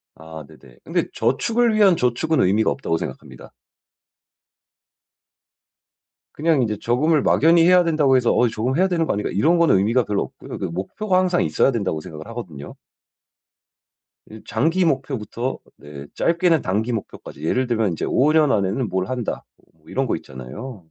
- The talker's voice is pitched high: No, low, 125 Hz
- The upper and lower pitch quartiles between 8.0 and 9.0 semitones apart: Yes, wide, 8.7 semitones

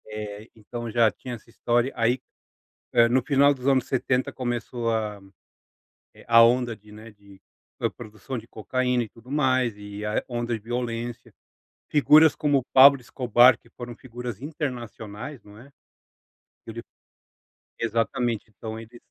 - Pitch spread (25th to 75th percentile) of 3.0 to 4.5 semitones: No, narrow, 2.5 semitones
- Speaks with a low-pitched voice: Yes, low, 120 Hz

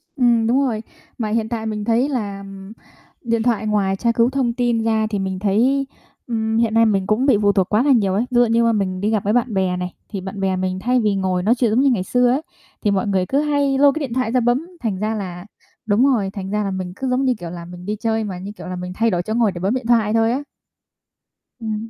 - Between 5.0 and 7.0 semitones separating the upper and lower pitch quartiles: No, average, 3.7 semitones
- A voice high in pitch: Yes, high, 220 Hz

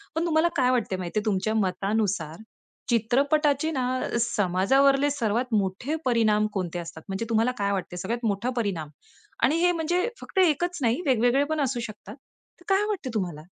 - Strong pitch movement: Yes, wide, 6.3 semitones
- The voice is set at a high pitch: Yes, high, 235 Hz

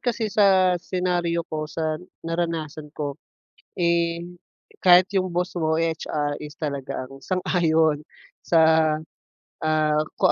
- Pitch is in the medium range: Yes, medium, 165 Hz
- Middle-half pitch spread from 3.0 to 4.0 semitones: No, narrow, 2.5 semitones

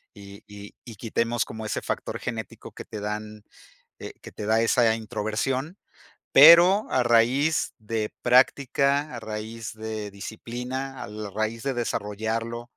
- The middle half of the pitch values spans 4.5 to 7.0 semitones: No, average, 2.9 semitones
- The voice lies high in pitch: No, low, 115 Hz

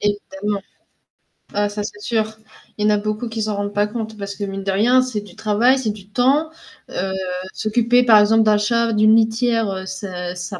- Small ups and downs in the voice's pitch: Yes, narrow, 2.0 semitones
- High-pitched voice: Yes, high, 215 Hz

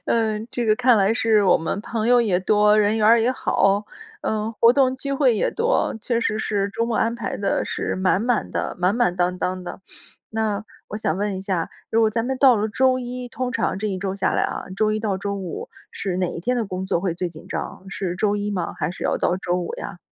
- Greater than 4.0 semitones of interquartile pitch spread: No, average, 3.5 semitones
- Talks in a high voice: Yes, high, 210 Hz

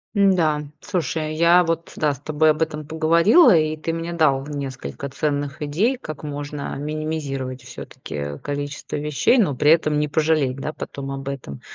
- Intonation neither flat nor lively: No, narrow, 2.3 semitones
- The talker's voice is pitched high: No, medium, 150 Hz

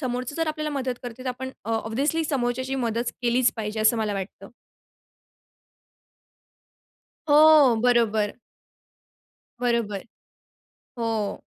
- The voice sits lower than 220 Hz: No, high, 245 Hz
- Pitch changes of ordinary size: Yes, average, 3.0 semitones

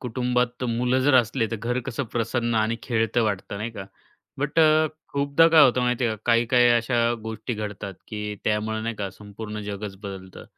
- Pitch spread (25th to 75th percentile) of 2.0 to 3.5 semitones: Yes, average, 2.7 semitones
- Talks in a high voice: No, low, 115 Hz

